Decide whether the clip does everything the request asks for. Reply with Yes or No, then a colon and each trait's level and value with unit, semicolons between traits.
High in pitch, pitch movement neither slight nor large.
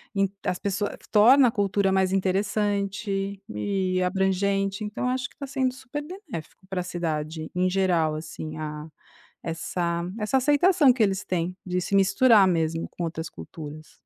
Yes: high, 195 Hz; average, 3.6 semitones